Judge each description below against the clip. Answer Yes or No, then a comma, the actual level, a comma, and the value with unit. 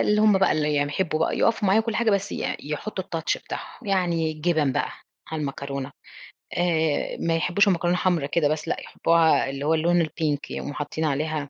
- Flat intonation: No, average, 3.5 semitones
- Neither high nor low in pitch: Yes, medium, 160 Hz